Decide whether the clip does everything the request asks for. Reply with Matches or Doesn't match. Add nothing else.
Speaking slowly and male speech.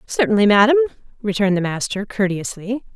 Doesn't match